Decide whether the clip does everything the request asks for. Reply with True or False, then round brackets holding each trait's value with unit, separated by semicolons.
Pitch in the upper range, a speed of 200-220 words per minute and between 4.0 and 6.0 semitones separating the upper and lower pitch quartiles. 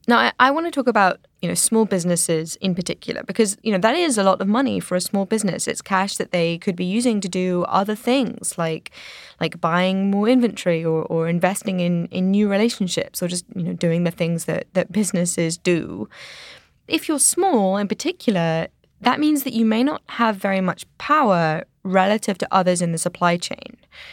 True (195 Hz; 205 wpm; 4.4 semitones)